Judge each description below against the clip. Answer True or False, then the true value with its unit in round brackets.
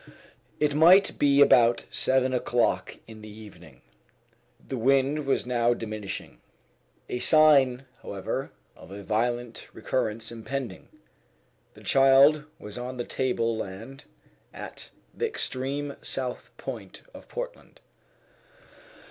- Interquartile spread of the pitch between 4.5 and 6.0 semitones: False (3.5 semitones)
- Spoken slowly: True (115 wpm)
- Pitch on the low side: True (125 Hz)